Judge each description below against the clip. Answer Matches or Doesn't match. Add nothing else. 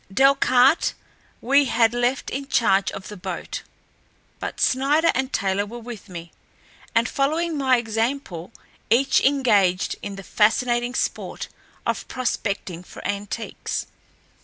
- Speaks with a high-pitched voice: Matches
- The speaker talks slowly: Matches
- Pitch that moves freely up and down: Doesn't match